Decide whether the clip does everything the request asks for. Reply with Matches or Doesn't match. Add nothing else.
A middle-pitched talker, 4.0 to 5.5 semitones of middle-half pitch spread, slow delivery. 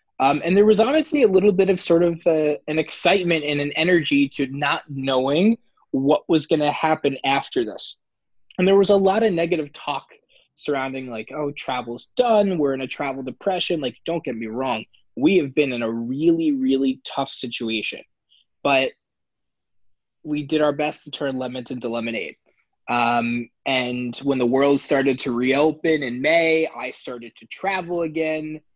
Doesn't match